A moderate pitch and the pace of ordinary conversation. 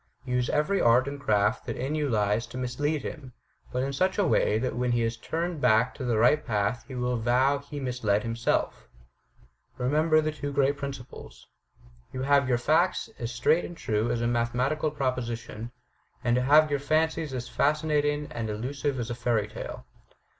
No: low, 130 Hz; average, 185 wpm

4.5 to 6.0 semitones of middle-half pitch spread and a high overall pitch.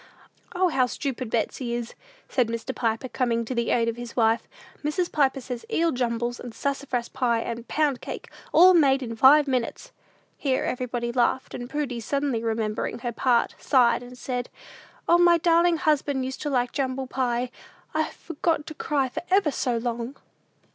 No: average, 3.4 semitones; very high, 255 Hz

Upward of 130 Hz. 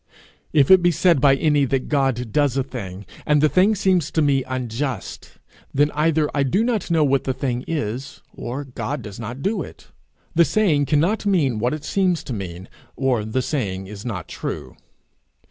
Yes: medium, 140 Hz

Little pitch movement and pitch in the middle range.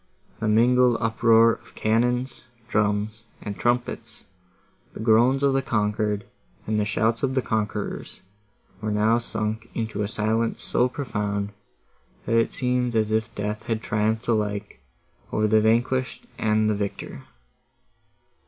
No: narrow, 1.9 semitones; low, 110 Hz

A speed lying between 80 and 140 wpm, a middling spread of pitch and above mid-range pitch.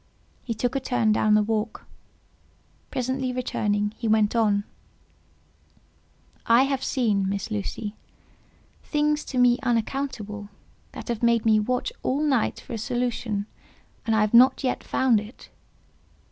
Yes: slow, 135 wpm; average, 3.1 semitones; high, 230 Hz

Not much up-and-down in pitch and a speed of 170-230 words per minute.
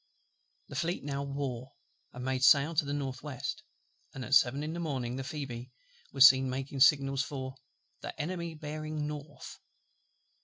No: narrow, 2.2 semitones; average, 160 wpm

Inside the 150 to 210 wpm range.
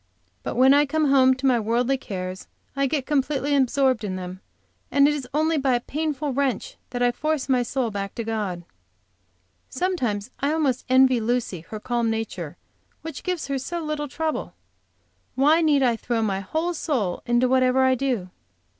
Yes: average, 175 wpm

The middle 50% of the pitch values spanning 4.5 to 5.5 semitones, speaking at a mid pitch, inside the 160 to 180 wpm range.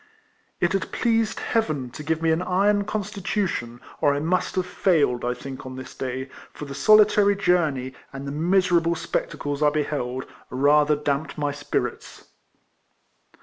No: average, 5.1 semitones; medium, 150 Hz; average, 150 wpm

